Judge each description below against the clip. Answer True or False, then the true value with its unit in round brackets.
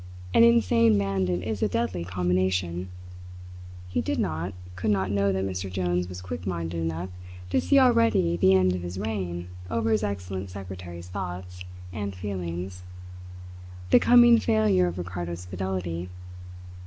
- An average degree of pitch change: False (2.0 semitones)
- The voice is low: True (95 Hz)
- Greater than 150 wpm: False (145 wpm)